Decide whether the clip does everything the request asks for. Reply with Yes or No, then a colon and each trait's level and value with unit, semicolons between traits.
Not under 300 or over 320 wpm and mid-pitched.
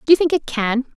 No: fast, 305 wpm; very high, 275 Hz